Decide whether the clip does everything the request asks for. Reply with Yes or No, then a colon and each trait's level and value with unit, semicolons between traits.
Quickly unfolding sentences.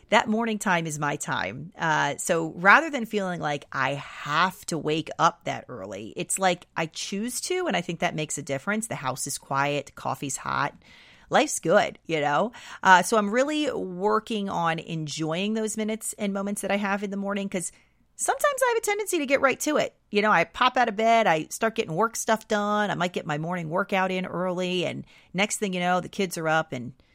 Yes: fast, 220 wpm